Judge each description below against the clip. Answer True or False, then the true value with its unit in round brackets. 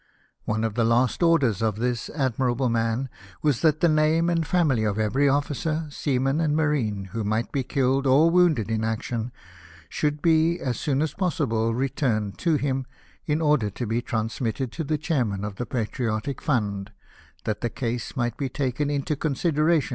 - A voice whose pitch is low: True (130 Hz)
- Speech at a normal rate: True (175 wpm)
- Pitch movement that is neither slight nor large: True (5.0 semitones)